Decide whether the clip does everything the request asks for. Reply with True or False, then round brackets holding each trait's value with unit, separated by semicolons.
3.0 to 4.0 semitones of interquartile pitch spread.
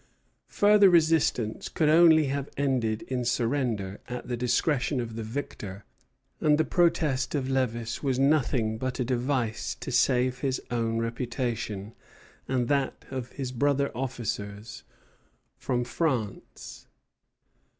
True (3.5 semitones)